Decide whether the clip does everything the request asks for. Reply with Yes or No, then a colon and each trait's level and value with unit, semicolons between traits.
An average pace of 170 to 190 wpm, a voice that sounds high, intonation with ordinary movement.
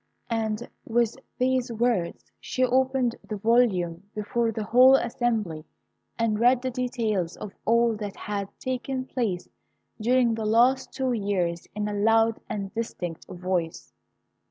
No: slow, 135 wpm; high, 225 Hz; average, 3.3 semitones